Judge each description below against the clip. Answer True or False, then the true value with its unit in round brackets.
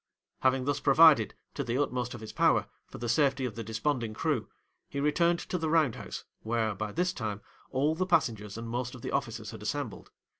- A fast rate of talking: True (210 wpm)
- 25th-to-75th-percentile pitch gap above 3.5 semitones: True (4.6 semitones)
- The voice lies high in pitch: False (130 Hz)